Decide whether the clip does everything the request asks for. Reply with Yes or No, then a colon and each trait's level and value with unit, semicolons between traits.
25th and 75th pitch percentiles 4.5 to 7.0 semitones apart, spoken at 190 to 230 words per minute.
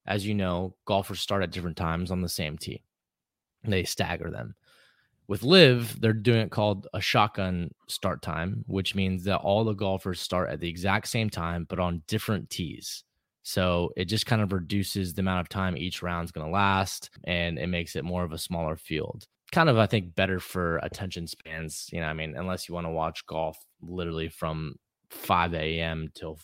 No: average, 3.0 semitones; average, 200 wpm